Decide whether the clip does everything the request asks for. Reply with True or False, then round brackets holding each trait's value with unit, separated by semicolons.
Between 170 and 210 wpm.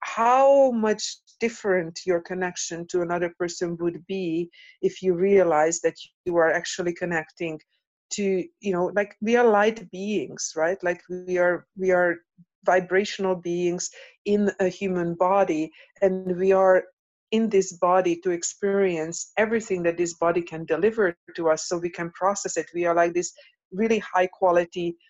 False (160 wpm)